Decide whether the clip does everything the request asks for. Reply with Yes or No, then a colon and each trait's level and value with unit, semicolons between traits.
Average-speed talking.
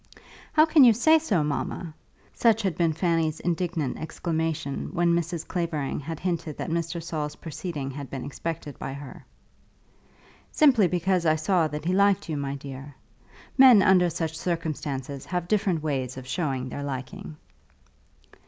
Yes: average, 155 wpm